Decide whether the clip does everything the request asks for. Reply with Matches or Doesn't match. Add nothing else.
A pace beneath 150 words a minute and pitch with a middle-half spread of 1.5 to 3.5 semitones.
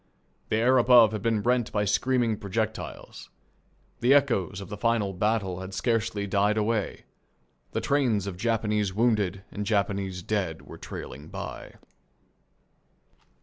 Matches